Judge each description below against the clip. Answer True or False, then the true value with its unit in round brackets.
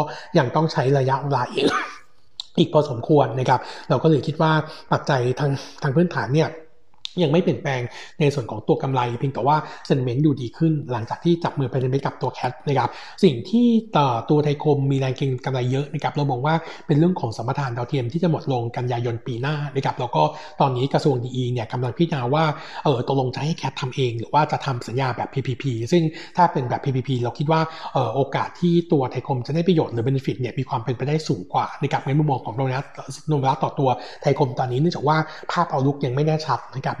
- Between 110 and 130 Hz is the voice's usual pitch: False (140 Hz)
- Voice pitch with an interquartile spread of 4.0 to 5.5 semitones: False (3.4 semitones)